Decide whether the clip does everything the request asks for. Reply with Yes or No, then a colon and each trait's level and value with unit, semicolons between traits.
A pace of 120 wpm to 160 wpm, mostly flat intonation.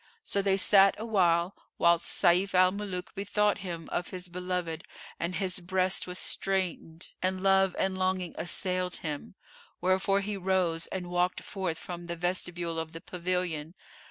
Yes: average, 155 wpm; narrow, 1.8 semitones